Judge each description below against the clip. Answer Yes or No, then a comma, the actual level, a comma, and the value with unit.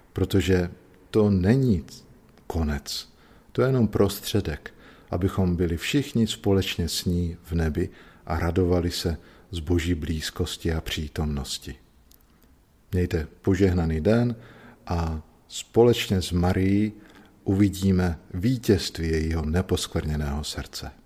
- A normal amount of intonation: Yes, average, 3.3 semitones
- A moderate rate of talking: No, slow, 105 wpm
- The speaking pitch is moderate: No, very low, 90 Hz